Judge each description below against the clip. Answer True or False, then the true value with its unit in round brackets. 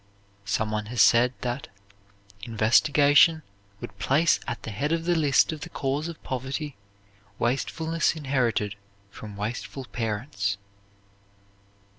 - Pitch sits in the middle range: False (130 Hz)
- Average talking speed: False (120 wpm)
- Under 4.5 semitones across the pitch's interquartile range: False (5.3 semitones)